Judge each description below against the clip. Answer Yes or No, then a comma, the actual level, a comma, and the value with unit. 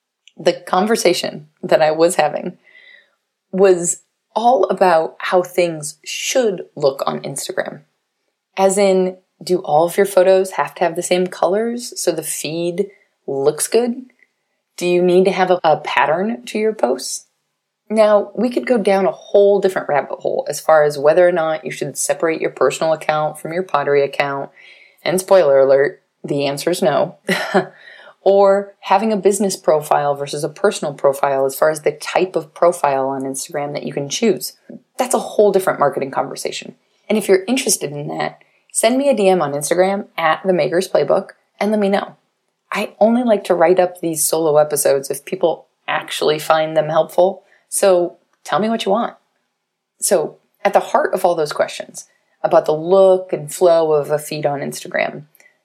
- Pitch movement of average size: Yes, average, 4.2 semitones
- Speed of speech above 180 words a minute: No, average, 175 wpm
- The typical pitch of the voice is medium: Yes, medium, 180 Hz